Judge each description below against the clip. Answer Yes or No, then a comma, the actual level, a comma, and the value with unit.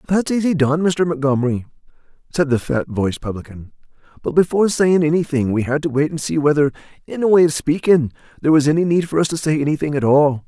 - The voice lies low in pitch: No, medium, 150 Hz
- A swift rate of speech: Yes, fast, 210 wpm